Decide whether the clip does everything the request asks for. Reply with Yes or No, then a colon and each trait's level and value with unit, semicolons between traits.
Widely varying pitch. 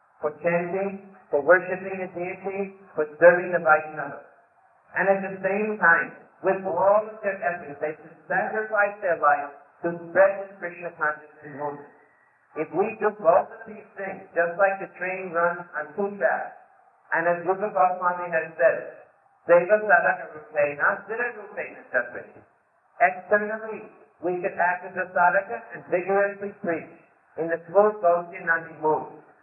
No: average, 3.1 semitones